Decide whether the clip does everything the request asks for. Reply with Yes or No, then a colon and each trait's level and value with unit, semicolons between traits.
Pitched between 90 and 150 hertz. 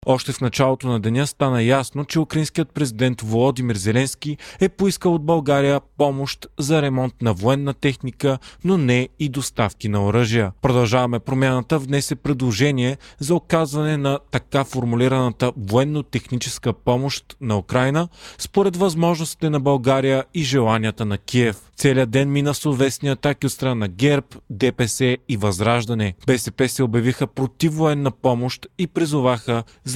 Yes: low, 135 Hz